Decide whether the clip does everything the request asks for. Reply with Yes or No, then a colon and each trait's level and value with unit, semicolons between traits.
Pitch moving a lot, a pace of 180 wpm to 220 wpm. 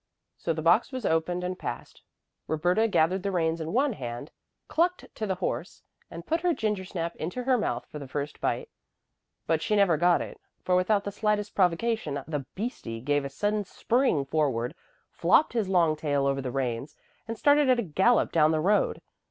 Yes: wide, 5.8 semitones; average, 190 wpm